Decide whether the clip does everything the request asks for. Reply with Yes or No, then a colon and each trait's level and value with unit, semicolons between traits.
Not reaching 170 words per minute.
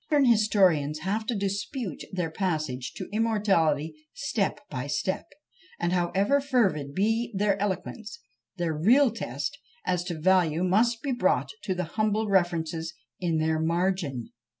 Yes: average, 140 wpm